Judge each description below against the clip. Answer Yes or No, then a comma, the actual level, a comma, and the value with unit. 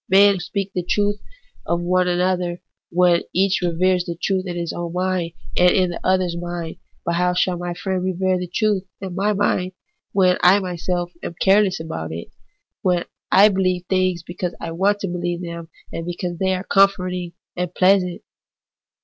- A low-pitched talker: No, medium, 180 Hz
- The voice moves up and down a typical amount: No, narrow, 1.4 semitones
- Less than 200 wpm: Yes, average, 175 wpm